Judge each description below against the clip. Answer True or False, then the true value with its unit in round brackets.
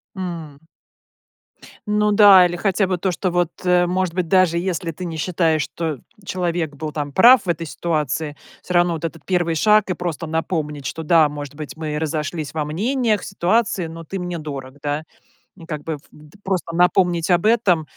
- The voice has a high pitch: False (170 Hz)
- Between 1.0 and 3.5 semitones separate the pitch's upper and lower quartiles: True (3.0 semitones)